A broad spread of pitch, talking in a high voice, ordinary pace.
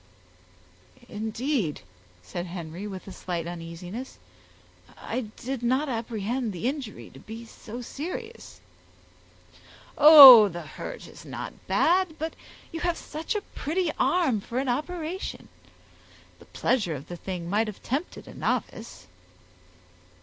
No: wide, 8.1 semitones; high, 235 Hz; slow, 130 wpm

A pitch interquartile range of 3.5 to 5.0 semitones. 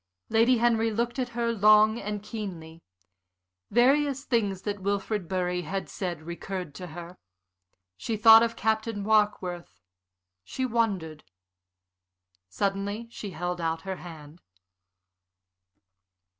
Yes: average, 4.3 semitones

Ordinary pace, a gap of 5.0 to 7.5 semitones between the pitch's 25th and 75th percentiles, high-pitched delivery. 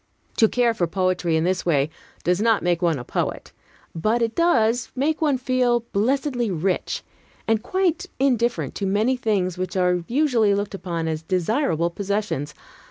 Yes: average, 165 wpm; wide, 5.5 semitones; high, 205 Hz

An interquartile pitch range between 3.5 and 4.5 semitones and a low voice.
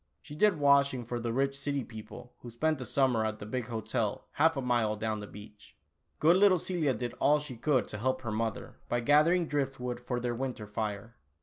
Yes: average, 4.1 semitones; low, 125 Hz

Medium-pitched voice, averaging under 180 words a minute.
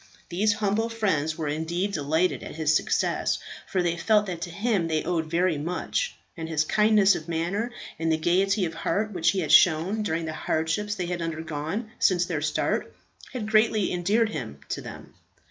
No: medium, 175 Hz; average, 185 wpm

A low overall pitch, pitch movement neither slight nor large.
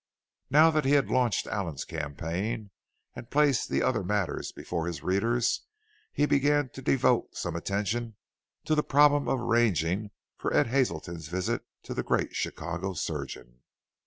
No: low, 110 Hz; wide, 7.6 semitones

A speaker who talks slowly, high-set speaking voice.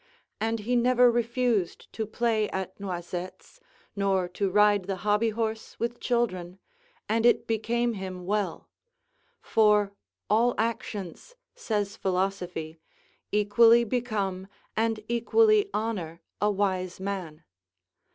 Yes: slow, 110 wpm; high, 210 Hz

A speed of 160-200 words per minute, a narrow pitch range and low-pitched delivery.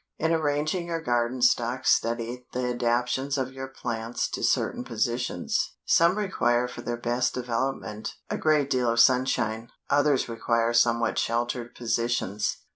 No: average, 140 wpm; narrow, 2.2 semitones; low, 120 Hz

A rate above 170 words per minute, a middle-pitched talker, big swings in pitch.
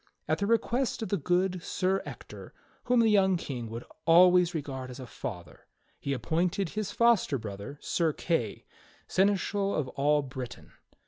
No: average, 165 wpm; medium, 170 Hz; wide, 6.7 semitones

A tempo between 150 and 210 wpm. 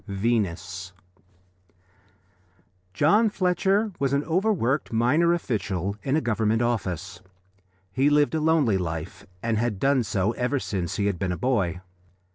No: slow, 135 wpm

